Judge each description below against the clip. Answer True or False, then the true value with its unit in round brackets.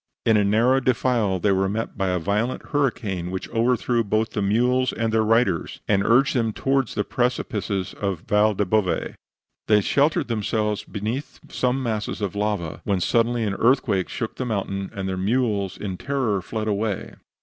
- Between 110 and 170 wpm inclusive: False (180 wpm)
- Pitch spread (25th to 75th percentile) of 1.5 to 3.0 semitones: False (3.5 semitones)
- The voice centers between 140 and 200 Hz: False (110 Hz)